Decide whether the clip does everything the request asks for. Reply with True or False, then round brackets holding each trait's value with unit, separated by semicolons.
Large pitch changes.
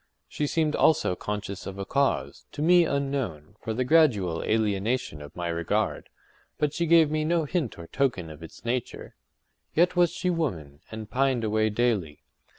True (8.1 semitones)